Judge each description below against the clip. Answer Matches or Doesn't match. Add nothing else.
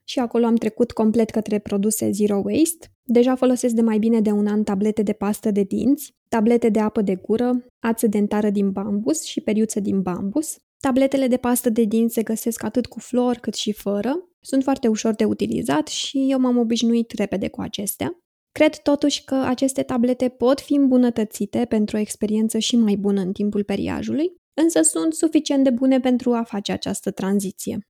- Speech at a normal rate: Doesn't match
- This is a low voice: Doesn't match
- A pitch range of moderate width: Matches